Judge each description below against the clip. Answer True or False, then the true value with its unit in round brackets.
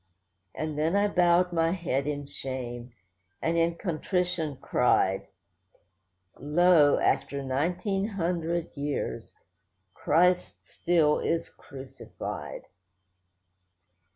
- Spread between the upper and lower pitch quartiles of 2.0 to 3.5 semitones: False (3.9 semitones)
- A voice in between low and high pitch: True (165 Hz)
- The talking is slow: True (90 wpm)